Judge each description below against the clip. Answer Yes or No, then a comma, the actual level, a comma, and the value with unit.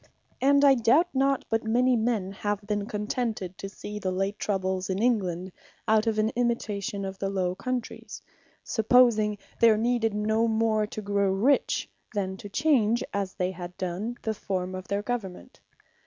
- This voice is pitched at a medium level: No, high, 210 Hz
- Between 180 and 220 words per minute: No, average, 170 wpm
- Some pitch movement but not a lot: Yes, average, 3.2 semitones